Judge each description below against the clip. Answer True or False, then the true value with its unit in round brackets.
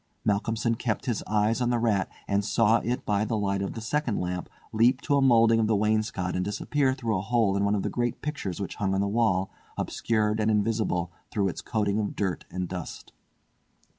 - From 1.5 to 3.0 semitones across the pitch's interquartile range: True (2.7 semitones)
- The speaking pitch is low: True (110 Hz)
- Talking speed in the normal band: False (215 wpm)